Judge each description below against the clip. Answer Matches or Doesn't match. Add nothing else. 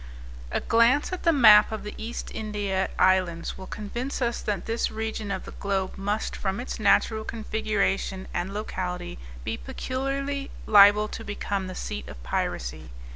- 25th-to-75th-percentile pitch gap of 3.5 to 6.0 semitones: Doesn't match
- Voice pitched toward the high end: Matches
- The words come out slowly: Doesn't match